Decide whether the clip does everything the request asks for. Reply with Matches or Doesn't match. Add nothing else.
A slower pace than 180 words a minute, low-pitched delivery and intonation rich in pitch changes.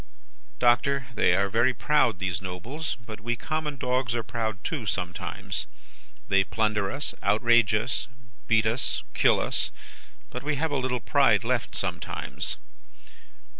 Doesn't match